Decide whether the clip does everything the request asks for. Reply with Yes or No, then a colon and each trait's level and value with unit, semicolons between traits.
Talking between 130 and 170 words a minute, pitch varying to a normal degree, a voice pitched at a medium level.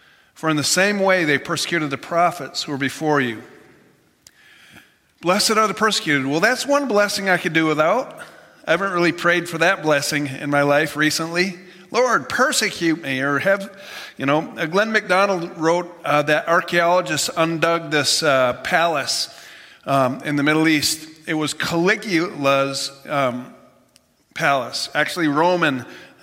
Yes: average, 150 wpm; average, 3.6 semitones; medium, 165 Hz